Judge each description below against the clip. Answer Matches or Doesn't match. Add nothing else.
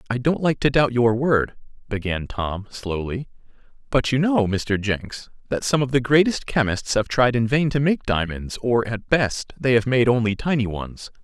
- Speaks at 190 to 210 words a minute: Matches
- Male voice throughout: Matches